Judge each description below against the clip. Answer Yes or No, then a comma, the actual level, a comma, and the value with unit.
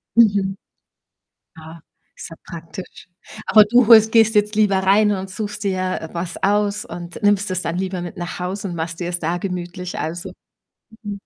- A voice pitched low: No, high, 190 Hz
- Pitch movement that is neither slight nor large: Yes, average, 3.0 semitones